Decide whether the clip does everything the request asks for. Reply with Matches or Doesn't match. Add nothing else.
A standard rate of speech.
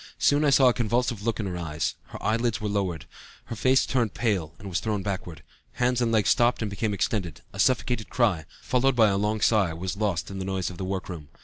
Doesn't match